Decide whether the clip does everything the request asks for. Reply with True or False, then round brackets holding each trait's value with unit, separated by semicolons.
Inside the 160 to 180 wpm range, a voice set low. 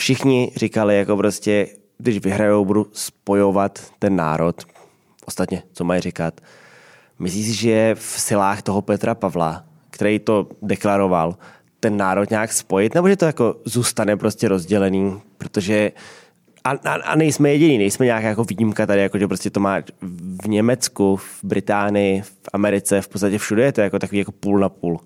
True (165 wpm; 100 Hz)